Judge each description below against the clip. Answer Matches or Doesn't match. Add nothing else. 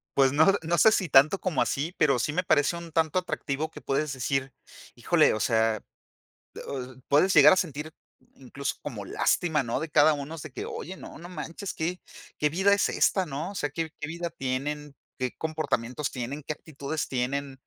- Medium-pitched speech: Matches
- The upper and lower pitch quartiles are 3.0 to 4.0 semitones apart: Matches